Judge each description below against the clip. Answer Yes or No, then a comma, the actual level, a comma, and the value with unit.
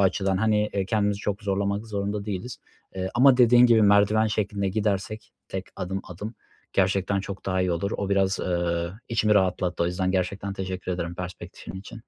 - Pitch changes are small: Yes, narrow, 2.3 semitones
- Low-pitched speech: Yes, low, 100 Hz